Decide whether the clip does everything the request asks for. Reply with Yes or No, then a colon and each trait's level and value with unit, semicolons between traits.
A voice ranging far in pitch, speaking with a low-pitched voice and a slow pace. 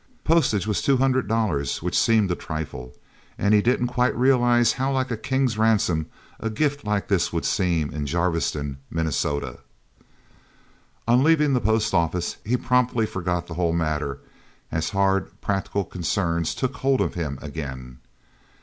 No: wide, 7.0 semitones; low, 100 Hz; average, 155 wpm